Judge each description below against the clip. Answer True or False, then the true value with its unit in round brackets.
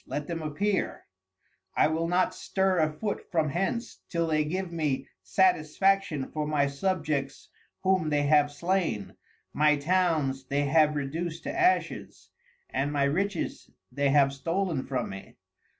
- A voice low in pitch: False (155 Hz)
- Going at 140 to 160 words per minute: True (145 wpm)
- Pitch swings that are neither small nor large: True (4.5 semitones)